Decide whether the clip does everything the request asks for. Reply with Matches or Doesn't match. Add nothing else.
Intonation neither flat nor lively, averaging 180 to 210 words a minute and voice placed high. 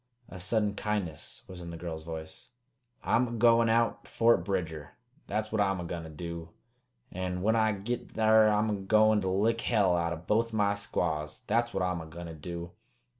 Doesn't match